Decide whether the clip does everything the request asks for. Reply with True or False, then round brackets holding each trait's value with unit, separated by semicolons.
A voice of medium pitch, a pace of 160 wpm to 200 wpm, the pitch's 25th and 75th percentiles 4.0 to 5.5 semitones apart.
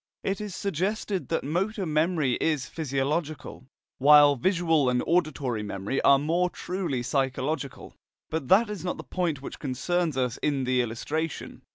False (150 Hz; 150 wpm; 4.9 semitones)